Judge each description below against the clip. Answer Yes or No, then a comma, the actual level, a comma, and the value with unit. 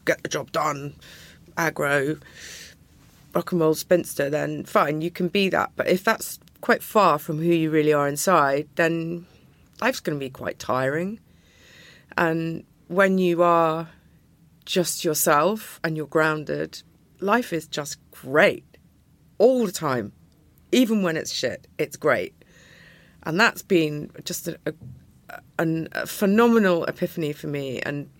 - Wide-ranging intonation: No, average, 3.0 semitones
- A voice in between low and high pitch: Yes, medium, 165 Hz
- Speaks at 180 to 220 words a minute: No, average, 145 wpm